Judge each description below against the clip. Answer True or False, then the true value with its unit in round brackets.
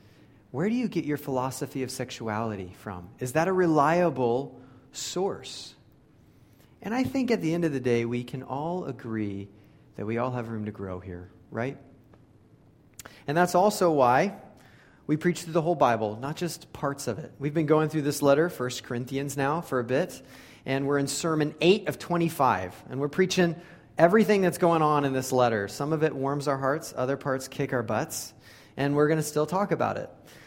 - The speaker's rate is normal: True (195 wpm)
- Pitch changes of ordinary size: True (4.7 semitones)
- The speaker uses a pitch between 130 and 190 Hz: True (140 Hz)